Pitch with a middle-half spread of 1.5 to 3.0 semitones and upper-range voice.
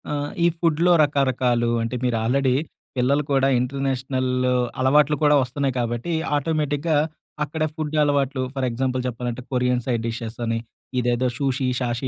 No: average, 2.7 semitones; low, 130 Hz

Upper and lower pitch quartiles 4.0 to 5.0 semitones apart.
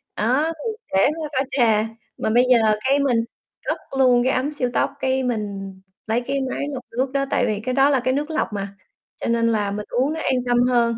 No: average, 3.4 semitones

